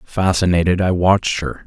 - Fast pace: No, average, 145 wpm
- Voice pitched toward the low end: Yes, very low, 90 Hz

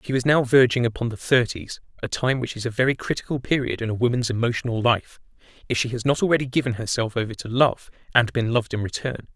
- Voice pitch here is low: Yes, low, 120 Hz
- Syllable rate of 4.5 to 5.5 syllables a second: No, 6.4 syllables/s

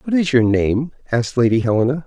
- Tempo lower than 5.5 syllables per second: No, 6.2 syllables/s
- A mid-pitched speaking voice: No, low, 130 Hz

